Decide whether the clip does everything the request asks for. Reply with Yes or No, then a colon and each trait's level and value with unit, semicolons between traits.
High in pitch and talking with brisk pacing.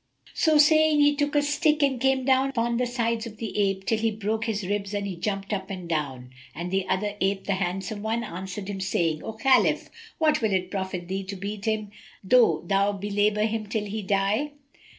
Yes: high, 210 Hz; fast, 210 wpm